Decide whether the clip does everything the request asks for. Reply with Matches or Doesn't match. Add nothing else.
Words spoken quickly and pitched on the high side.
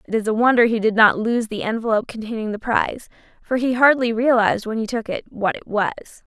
Matches